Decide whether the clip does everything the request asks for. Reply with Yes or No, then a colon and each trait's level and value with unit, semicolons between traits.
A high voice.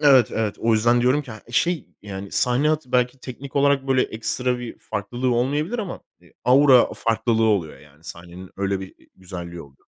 No: low, 120 Hz